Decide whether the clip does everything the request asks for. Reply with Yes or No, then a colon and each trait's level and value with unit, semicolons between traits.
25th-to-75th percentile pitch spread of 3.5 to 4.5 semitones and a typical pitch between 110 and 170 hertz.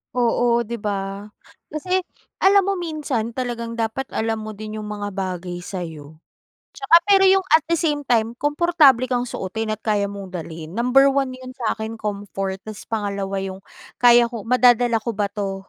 No: average, 4.2 semitones; high, 225 Hz